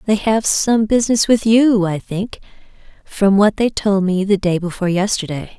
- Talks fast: No, average, 185 wpm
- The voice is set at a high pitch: Yes, high, 205 Hz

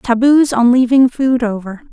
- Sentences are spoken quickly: No, average, 155 wpm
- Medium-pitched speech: No, high, 245 Hz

